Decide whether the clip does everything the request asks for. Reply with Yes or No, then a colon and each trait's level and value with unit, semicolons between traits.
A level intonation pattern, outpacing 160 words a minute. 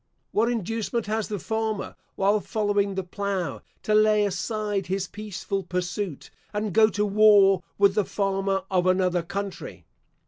No: narrow, 1.8 semitones; average, 145 wpm